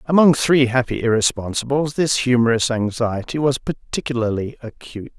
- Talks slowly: Yes, slow, 115 wpm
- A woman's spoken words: No, male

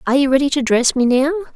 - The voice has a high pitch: Yes, very high, 275 Hz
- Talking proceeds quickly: Yes, fast, 270 wpm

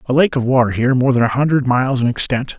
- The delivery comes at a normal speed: No, fast, 280 wpm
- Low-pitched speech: Yes, low, 130 Hz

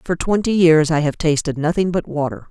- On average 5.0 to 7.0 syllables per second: Yes, 5.4 syllables/s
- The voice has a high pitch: No, medium, 160 Hz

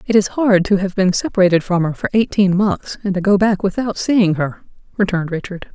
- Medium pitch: No, high, 195 Hz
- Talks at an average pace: No, fast, 220 wpm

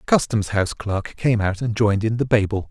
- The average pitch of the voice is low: Yes, low, 105 Hz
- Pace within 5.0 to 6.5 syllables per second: Yes, 5.7 syllables/s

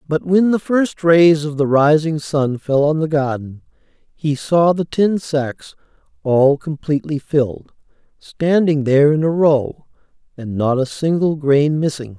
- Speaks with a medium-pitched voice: Yes, medium, 150 Hz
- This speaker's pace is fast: No, average, 160 wpm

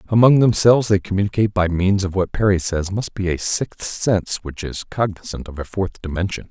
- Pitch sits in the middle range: No, very low, 95 Hz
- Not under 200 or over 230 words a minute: Yes, fast, 205 wpm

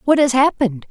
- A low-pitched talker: No, very high, 250 Hz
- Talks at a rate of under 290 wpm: Yes, average, 200 wpm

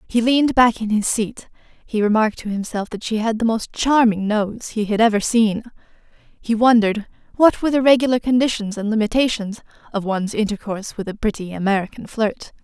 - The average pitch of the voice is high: Yes, high, 220 Hz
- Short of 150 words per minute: No, average, 180 wpm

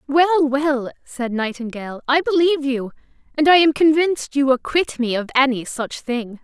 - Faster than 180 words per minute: No, average, 170 wpm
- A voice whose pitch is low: No, very high, 275 Hz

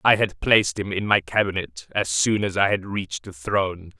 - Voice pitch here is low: Yes, very low, 95 Hz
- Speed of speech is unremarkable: No, fast, 225 wpm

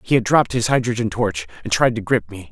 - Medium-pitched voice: No, low, 110 Hz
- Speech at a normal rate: No, fast, 265 wpm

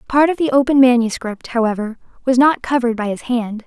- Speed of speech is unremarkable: Yes, average, 195 wpm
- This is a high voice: Yes, high, 245 Hz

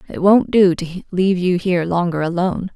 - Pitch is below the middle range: No, medium, 180 Hz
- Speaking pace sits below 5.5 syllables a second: No, 5.6 syllables/s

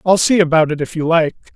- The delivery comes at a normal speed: No, fast, 270 wpm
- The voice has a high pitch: No, medium, 165 Hz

